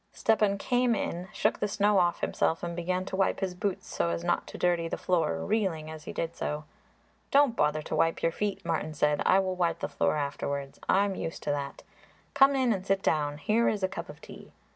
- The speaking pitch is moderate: Yes, medium, 180 Hz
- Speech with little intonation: No, average, 4.5 semitones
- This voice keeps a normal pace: No, fast, 230 wpm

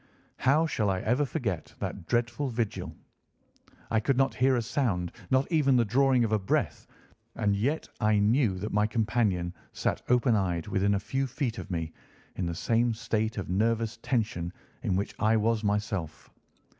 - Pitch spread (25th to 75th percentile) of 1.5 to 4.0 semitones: Yes, average, 3.7 semitones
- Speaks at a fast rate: No, average, 175 wpm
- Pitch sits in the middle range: No, low, 110 Hz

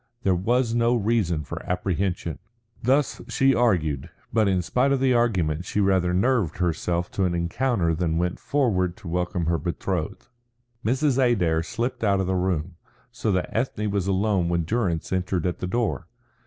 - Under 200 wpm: Yes, average, 170 wpm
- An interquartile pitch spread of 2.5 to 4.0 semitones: No, average, 5.2 semitones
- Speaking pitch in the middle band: No, very low, 95 Hz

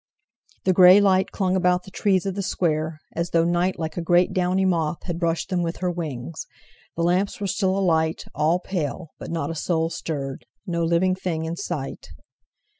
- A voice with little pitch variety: Yes, narrow, 2.3 semitones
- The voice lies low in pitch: No, medium, 175 Hz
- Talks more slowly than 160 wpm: No, average, 190 wpm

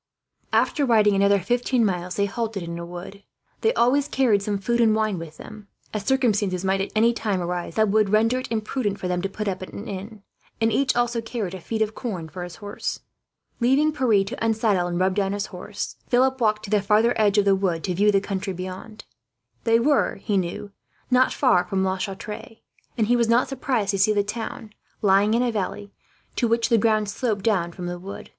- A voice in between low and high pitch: No, high, 210 Hz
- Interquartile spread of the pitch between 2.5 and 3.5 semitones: Yes, average, 3.1 semitones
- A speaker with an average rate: No, fast, 220 wpm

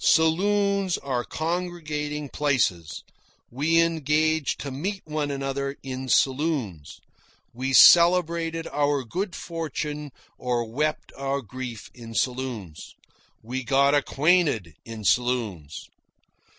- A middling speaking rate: No, slow, 100 wpm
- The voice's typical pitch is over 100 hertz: Yes, medium, 140 Hz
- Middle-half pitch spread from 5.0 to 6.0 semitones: No, average, 4.4 semitones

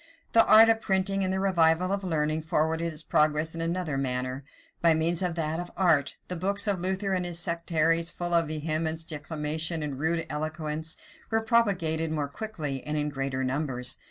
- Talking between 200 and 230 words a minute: No, average, 185 wpm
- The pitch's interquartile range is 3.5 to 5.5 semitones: No, average, 3.1 semitones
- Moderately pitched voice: Yes, medium, 165 Hz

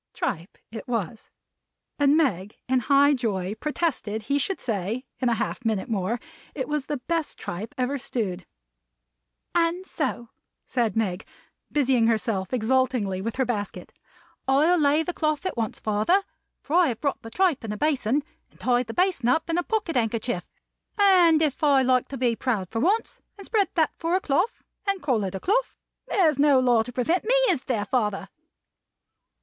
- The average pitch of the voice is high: Yes, very high, 255 Hz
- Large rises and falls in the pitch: Yes, wide, 5.9 semitones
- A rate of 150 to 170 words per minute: No, average, 180 wpm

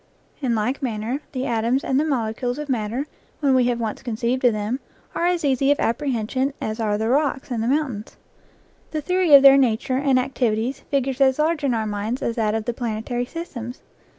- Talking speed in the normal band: No, fast, 230 wpm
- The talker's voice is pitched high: Yes, very high, 250 Hz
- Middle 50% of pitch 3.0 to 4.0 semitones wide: Yes, average, 3.5 semitones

